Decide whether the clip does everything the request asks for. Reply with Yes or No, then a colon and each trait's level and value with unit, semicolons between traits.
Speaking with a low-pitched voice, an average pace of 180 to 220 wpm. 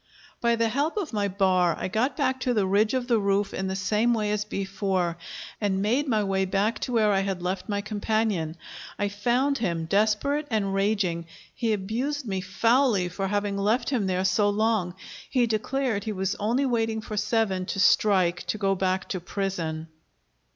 No: high, 205 Hz; average, 190 wpm